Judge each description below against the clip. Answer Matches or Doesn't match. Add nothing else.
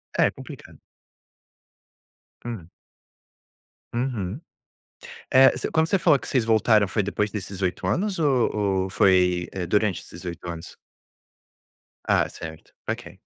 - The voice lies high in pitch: Doesn't match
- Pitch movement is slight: Doesn't match